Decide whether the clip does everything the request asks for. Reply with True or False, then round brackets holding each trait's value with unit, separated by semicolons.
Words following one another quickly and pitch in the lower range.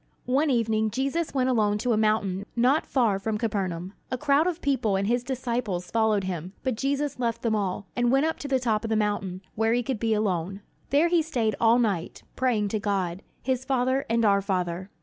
False (210 wpm; 225 Hz)